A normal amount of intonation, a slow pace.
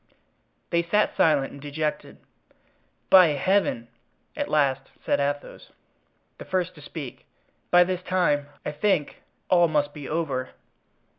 Yes: average, 4.0 semitones; slow, 130 wpm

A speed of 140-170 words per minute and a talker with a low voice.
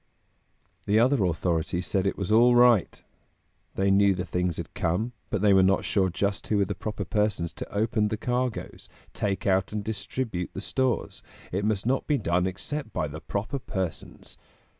No: average, 180 wpm; low, 100 Hz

